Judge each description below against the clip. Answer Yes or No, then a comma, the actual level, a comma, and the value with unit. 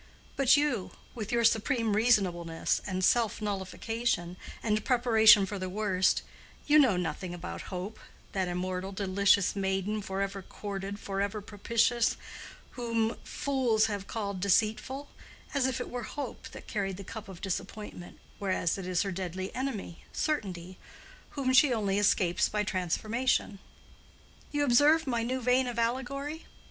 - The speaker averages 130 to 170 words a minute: Yes, average, 140 wpm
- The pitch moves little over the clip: No, average, 4.0 semitones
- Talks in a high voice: Yes, high, 210 Hz